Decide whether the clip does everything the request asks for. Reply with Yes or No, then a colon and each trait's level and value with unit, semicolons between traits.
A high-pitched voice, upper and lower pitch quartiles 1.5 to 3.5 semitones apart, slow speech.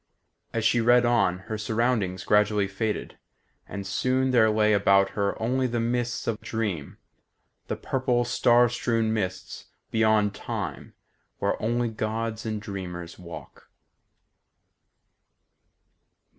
No: low, 110 Hz; average, 2.8 semitones; slow, 115 wpm